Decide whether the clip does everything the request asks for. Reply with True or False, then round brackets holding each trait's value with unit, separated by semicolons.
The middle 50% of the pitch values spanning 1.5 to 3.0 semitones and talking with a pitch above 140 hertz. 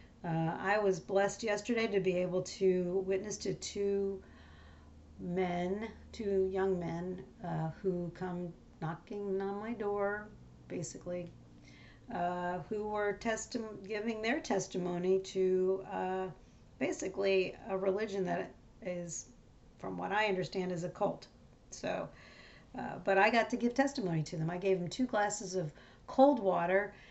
True (2.5 semitones; 190 Hz)